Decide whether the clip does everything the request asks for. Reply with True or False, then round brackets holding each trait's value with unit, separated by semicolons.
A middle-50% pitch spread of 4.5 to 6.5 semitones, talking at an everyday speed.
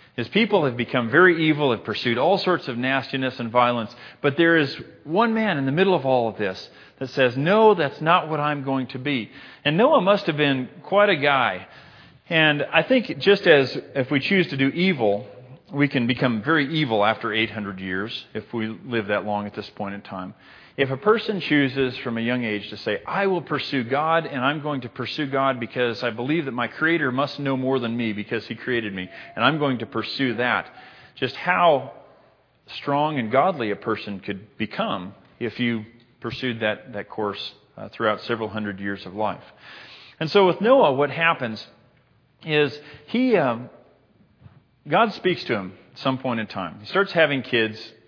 True (5.3 semitones; 195 wpm)